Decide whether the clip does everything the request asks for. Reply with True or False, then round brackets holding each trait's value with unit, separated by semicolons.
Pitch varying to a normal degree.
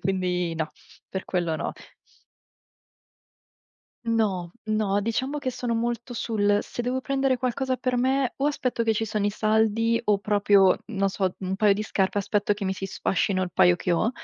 True (3.7 semitones)